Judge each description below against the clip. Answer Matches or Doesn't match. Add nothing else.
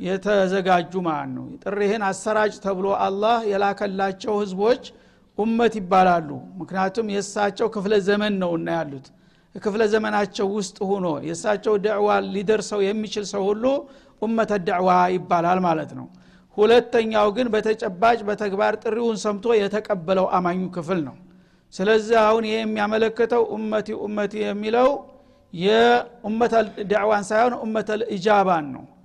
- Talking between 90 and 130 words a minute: Matches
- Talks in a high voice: Matches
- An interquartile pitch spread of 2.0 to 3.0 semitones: Matches